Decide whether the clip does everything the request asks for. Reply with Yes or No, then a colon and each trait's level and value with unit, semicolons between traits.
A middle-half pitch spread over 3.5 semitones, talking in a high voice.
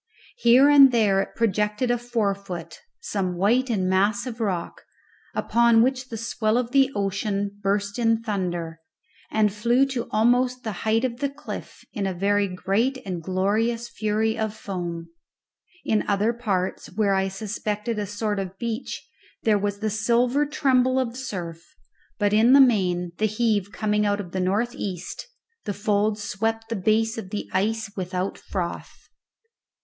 No: average, 3.2 semitones; high, 215 Hz